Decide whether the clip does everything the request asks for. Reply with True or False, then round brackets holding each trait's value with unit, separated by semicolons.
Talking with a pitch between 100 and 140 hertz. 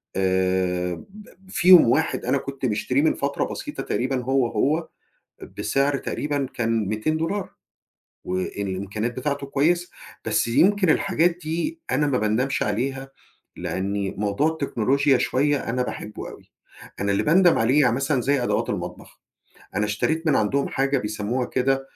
True (135 Hz)